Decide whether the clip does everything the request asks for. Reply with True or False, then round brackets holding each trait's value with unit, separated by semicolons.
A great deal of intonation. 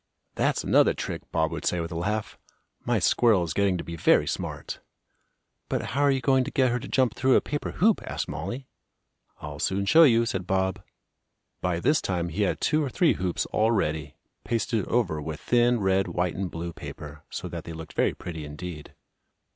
True (6.5 semitones)